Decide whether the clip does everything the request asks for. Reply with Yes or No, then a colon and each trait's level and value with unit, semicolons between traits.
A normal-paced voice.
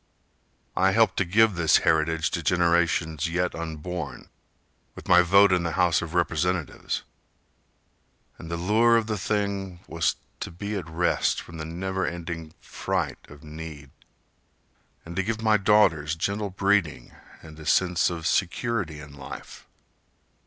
Yes: average, 145 wpm